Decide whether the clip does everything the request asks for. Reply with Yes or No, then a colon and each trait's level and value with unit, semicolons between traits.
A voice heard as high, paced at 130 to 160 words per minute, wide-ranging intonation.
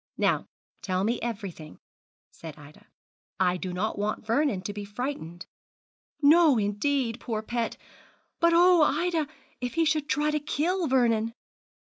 Yes: high, 235 Hz; average, 140 wpm; wide, 6.8 semitones